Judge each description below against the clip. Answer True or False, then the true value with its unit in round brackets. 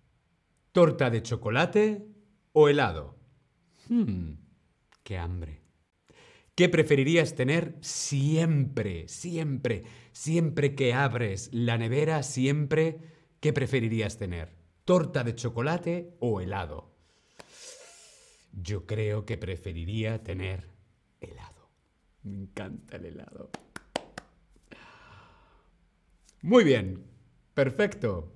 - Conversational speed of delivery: False (85 wpm)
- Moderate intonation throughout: False (7.9 semitones)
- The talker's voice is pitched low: True (125 Hz)